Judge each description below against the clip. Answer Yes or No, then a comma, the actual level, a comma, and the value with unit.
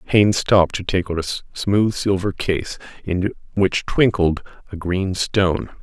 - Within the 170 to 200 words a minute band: No, average, 155 wpm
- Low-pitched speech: Yes, very low, 95 Hz